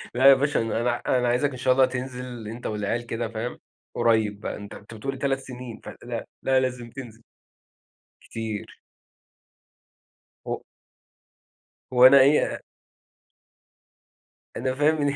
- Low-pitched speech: Yes, low, 125 Hz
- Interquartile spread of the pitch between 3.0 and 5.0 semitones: No, narrow, 2.6 semitones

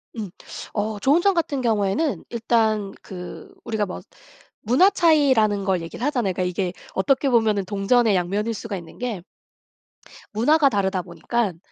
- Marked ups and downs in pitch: No, average, 4.5 semitones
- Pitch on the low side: No, high, 215 Hz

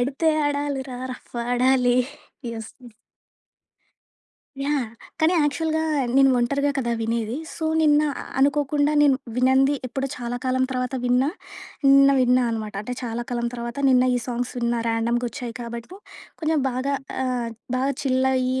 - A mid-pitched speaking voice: No, very high, 255 Hz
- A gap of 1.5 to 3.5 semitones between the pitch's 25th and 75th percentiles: Yes, narrow, 2.6 semitones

